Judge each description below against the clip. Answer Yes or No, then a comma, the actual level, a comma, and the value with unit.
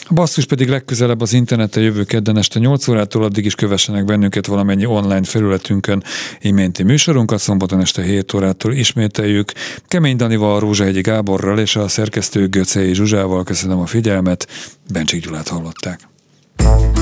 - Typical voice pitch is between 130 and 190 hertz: No, low, 105 Hz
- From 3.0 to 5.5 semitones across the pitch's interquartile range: No, narrow, 2.5 semitones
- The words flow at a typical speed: Yes, average, 140 wpm